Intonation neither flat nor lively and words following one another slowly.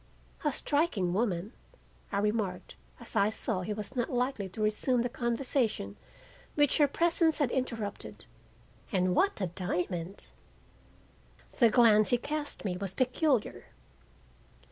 Yes: average, 5.0 semitones; slow, 130 wpm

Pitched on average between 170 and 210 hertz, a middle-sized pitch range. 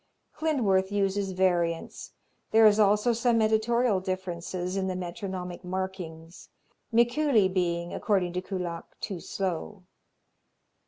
Yes: high, 190 Hz; average, 3.2 semitones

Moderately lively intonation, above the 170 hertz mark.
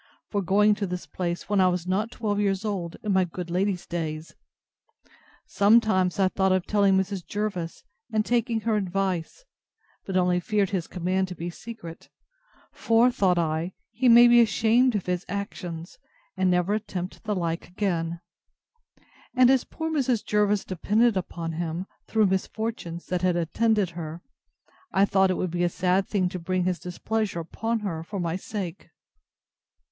Yes: average, 3.2 semitones; high, 190 Hz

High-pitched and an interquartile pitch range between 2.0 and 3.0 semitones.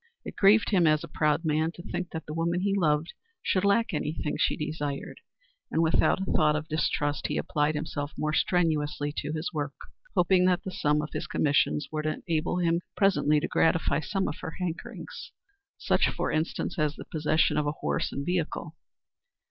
No: medium, 155 Hz; average, 2.7 semitones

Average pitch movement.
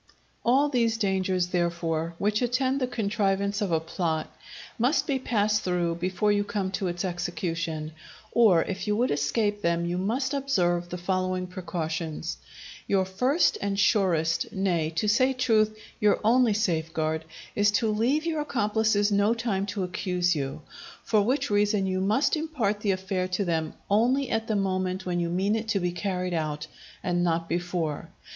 Yes: average, 3.8 semitones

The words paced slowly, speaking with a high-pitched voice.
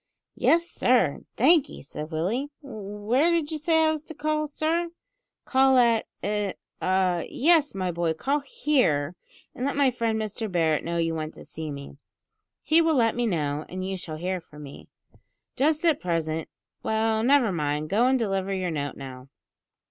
No: average, 180 wpm; high, 215 Hz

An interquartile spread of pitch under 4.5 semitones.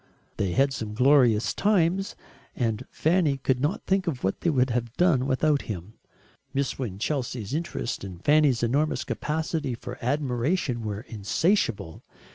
No: average, 5.0 semitones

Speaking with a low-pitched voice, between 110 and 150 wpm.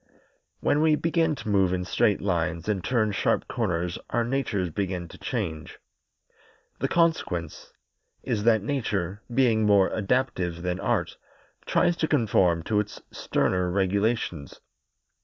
Yes: low, 100 Hz; slow, 135 wpm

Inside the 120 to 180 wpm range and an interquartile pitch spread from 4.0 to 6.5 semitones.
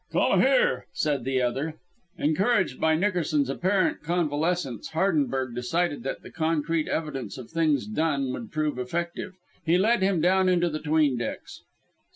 Yes: average, 150 wpm; average, 4.3 semitones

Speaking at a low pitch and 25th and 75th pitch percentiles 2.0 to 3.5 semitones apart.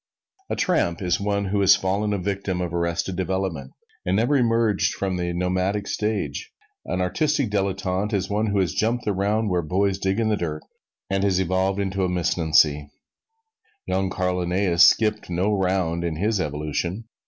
Yes: very low, 95 Hz; narrow, 2.4 semitones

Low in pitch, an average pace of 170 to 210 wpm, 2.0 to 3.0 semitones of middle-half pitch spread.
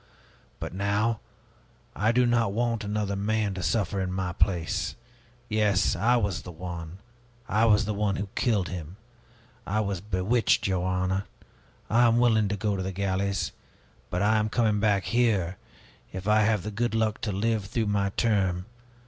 Yes: low, 100 Hz; average, 175 wpm; average, 2.7 semitones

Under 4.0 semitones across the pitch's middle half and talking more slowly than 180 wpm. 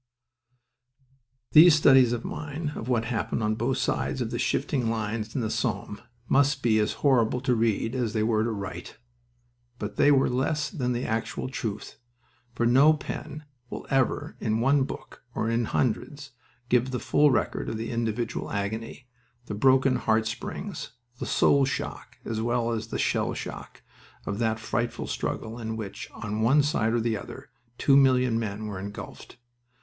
Yes: average, 3.3 semitones; average, 170 wpm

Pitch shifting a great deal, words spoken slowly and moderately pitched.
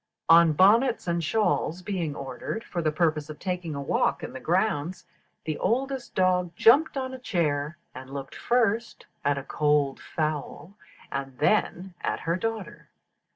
No: wide, 6.0 semitones; average, 155 wpm; medium, 170 Hz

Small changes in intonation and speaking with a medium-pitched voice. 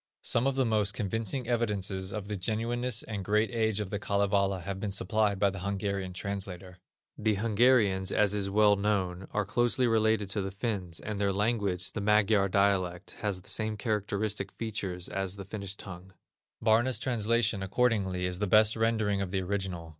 No: narrow, 2.2 semitones; low, 100 Hz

